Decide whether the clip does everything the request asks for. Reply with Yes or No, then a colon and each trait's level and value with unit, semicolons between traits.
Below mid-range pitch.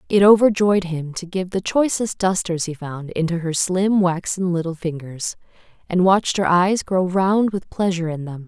No: medium, 180 Hz